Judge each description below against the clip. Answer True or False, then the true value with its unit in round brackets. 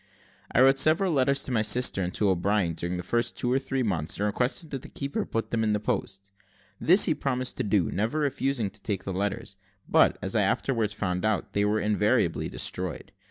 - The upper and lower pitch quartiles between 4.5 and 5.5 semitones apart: True (5.1 semitones)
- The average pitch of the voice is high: False (110 Hz)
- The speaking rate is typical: False (215 wpm)